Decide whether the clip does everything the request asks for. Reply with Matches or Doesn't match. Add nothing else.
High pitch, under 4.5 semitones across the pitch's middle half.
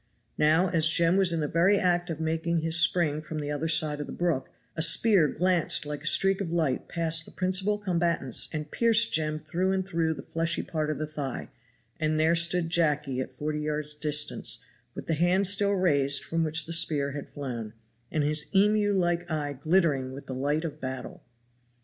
Doesn't match